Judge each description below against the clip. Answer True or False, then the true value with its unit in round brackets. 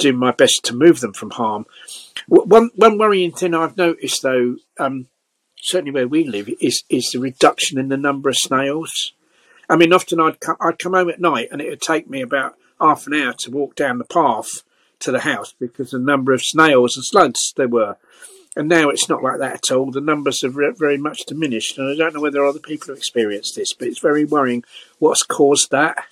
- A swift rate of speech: True (225 wpm)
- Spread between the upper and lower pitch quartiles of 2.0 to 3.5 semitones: False (4.0 semitones)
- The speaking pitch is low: False (145 Hz)